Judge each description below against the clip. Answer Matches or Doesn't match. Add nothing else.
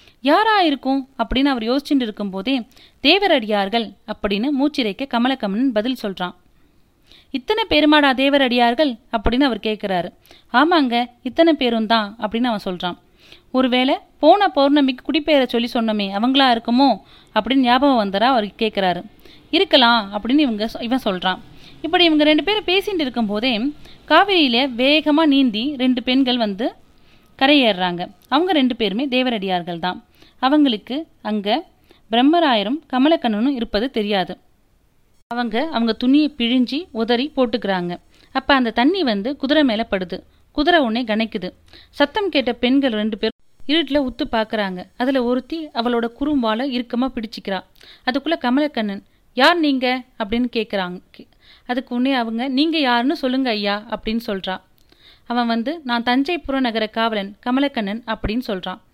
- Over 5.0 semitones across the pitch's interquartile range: Doesn't match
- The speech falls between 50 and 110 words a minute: Doesn't match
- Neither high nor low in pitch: Doesn't match